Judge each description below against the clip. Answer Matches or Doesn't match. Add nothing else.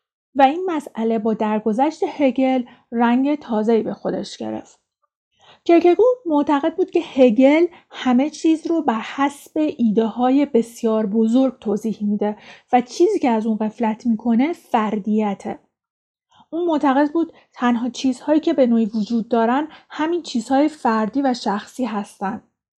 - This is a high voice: Matches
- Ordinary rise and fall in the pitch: Matches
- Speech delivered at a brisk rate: Doesn't match